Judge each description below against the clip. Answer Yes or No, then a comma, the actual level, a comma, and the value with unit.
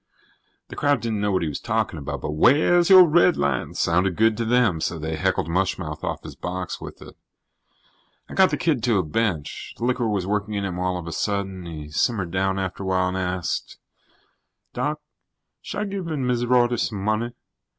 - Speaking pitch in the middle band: No, low, 100 Hz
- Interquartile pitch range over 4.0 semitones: Yes, average, 5.1 semitones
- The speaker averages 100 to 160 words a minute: No, average, 200 wpm